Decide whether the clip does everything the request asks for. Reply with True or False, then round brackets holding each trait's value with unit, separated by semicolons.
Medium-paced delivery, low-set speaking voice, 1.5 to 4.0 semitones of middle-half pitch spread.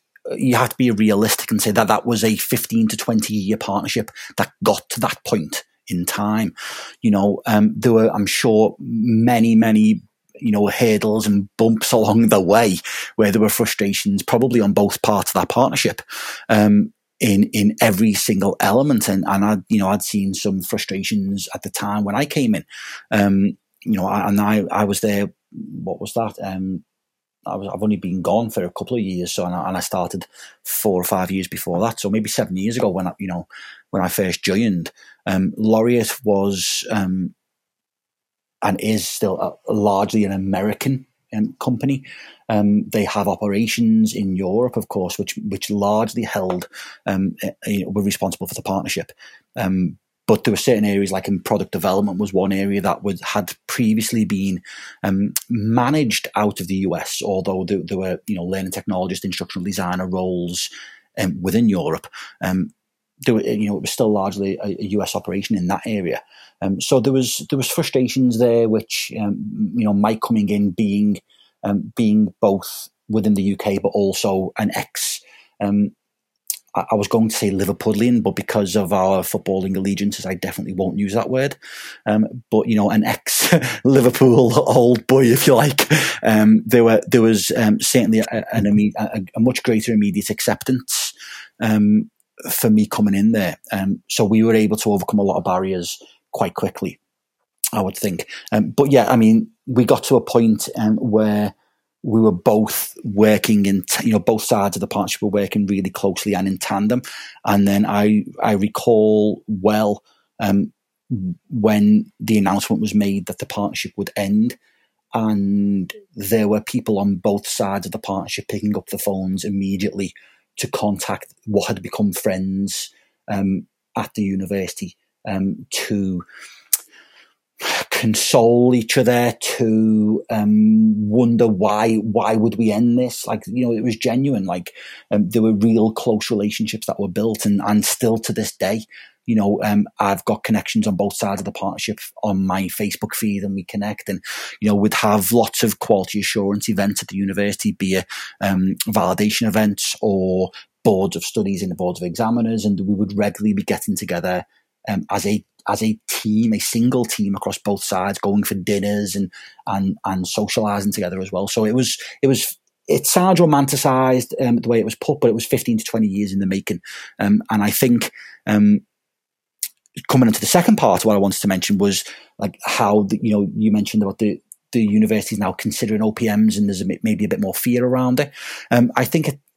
True (185 wpm; 105 Hz; 2.8 semitones)